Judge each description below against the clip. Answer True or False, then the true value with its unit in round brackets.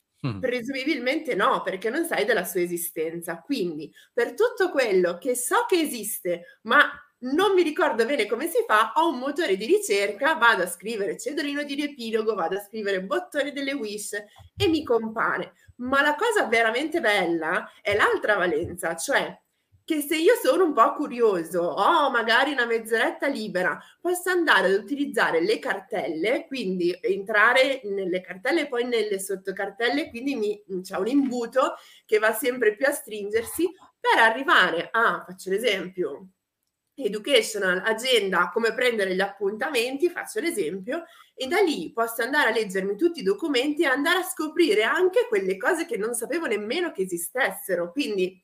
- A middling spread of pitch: False (8.5 semitones)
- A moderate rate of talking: True (160 wpm)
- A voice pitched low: False (255 Hz)